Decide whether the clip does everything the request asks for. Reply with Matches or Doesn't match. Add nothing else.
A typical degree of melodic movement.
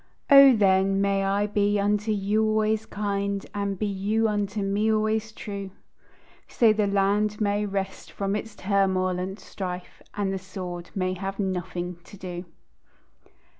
Doesn't match